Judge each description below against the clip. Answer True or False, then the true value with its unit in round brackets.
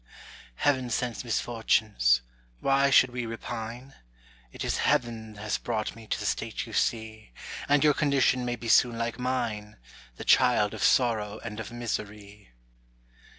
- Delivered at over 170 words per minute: False (150 wpm)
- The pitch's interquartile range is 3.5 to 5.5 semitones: False (2.6 semitones)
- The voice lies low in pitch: True (115 Hz)